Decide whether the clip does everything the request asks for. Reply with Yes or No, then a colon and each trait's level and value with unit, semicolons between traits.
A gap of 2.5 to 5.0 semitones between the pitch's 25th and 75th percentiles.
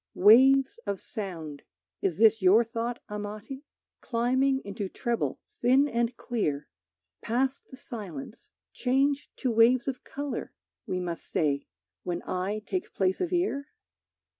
No: wide, 5.4 semitones